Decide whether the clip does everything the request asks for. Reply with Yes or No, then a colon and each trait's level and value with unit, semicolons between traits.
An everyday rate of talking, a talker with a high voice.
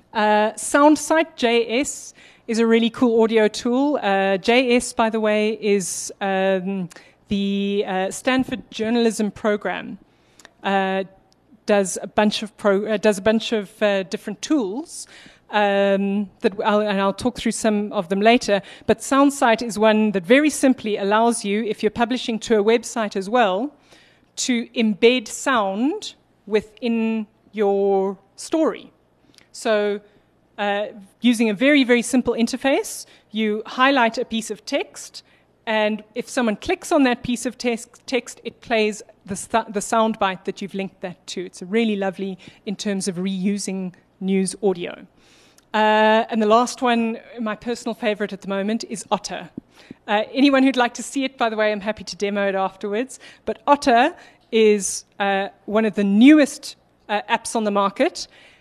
Yes: average, 160 wpm; high, 220 Hz